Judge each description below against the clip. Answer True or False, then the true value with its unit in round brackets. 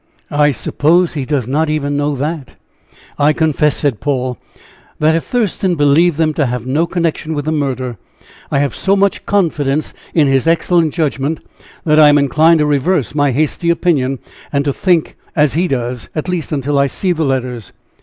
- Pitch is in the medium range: True (150 Hz)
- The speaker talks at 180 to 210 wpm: True (185 wpm)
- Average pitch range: True (3.0 semitones)